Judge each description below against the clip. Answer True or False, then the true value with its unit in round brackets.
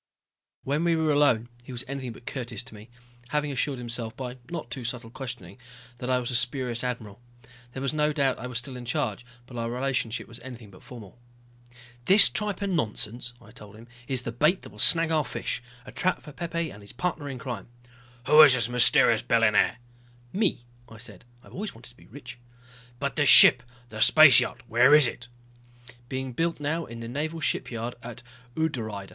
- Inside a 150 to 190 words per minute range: False (200 wpm)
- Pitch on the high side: False (125 Hz)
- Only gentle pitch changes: False (4.1 semitones)